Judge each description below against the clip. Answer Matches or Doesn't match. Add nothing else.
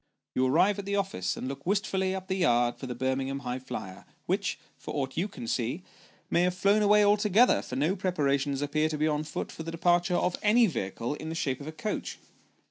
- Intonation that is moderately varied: Doesn't match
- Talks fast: Matches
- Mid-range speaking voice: Matches